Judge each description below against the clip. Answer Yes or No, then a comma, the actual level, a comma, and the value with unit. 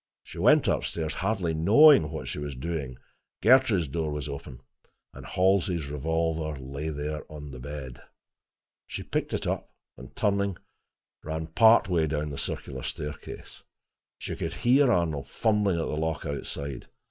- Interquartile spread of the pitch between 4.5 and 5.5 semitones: No, average, 4.0 semitones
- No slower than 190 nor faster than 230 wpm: No, average, 155 wpm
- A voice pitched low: Yes, very low, 80 Hz